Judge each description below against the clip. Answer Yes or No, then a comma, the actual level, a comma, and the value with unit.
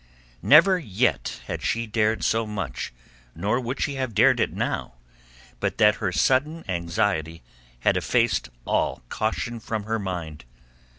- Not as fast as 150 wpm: Yes, average, 140 wpm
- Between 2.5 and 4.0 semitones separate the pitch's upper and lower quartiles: No, average, 5.1 semitones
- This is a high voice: No, low, 110 Hz